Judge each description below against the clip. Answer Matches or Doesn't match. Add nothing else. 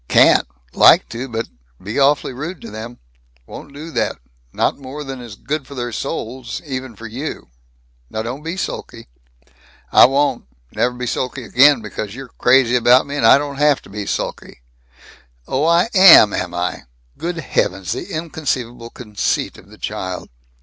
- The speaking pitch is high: Doesn't match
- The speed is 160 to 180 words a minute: Matches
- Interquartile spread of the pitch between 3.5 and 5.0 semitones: Matches